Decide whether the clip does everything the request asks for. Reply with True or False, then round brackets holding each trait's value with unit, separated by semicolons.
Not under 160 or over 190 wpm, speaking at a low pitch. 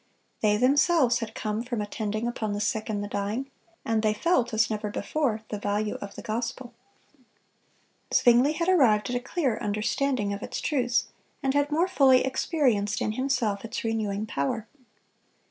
False (165 wpm; 230 Hz)